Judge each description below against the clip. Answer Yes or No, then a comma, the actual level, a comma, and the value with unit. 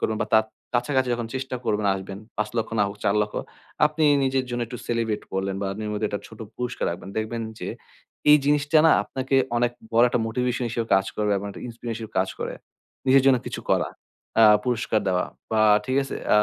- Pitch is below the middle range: Yes, low, 115 Hz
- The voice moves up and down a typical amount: Yes, average, 3.4 semitones